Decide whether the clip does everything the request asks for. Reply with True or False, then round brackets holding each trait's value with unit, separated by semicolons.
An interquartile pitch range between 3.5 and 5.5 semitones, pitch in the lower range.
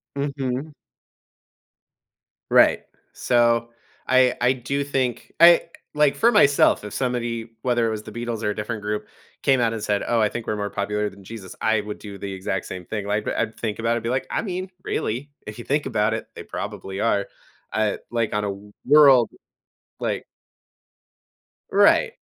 True (3.8 semitones; 115 Hz)